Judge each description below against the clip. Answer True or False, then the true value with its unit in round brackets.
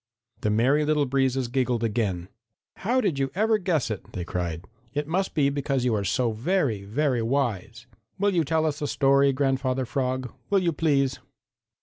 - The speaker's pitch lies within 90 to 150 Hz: True (135 Hz)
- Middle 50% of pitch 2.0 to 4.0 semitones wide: False (4.4 semitones)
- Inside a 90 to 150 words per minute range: False (180 wpm)